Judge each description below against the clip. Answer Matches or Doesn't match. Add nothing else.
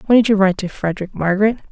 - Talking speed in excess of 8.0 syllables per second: Matches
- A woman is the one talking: Matches